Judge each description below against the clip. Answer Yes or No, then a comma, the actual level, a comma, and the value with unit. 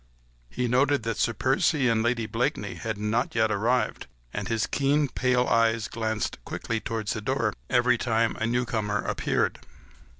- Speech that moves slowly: No, average, 160 wpm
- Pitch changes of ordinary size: No, narrow, 2.1 semitones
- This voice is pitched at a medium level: No, low, 115 Hz